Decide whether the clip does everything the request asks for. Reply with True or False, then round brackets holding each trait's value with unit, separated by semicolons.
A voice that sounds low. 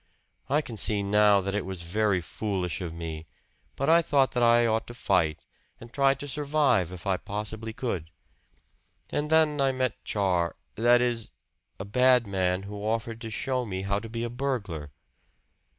True (110 Hz)